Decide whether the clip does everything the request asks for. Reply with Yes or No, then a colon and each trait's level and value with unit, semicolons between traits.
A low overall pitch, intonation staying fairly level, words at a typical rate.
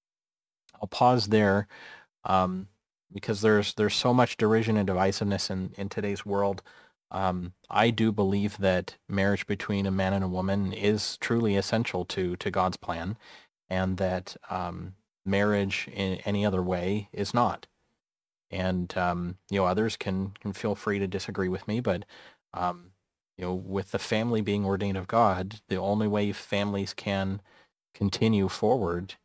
Yes: low, 100 Hz; narrow, 1.9 semitones; average, 155 wpm